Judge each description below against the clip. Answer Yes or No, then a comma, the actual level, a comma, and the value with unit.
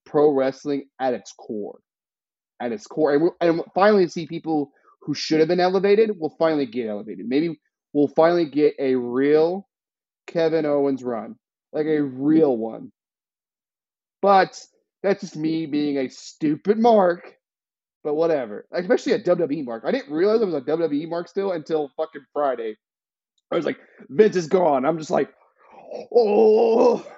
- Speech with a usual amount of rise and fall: Yes, average, 4.7 semitones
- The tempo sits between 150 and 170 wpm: Yes, average, 160 wpm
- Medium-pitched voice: Yes, medium, 160 Hz